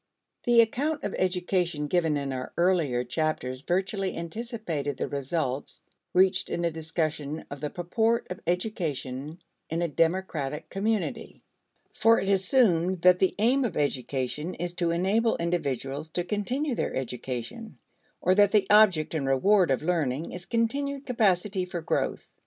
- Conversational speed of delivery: Yes, average, 145 wpm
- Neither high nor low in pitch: Yes, medium, 175 Hz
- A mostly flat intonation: No, wide, 5.4 semitones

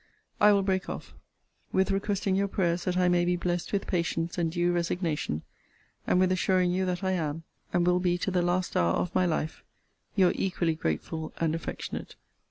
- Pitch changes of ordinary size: No, narrow, 1.8 semitones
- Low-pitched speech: No, medium, 180 Hz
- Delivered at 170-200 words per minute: Yes, average, 195 wpm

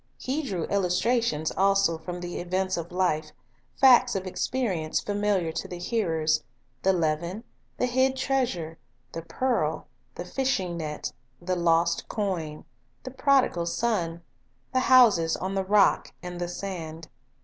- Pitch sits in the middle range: Yes, medium, 180 Hz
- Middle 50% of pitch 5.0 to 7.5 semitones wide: Yes, wide, 5.4 semitones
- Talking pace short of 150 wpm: Yes, average, 140 wpm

